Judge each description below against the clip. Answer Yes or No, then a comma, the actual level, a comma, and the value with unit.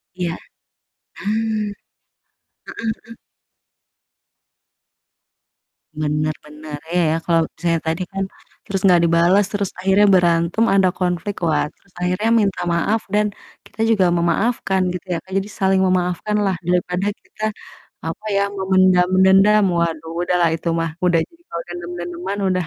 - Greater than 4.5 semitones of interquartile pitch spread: No, average, 2.7 semitones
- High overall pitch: No, medium, 180 Hz